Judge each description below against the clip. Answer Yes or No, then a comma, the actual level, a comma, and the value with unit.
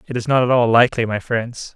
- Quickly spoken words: Yes, fast, 275 wpm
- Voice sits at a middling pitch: No, low, 120 Hz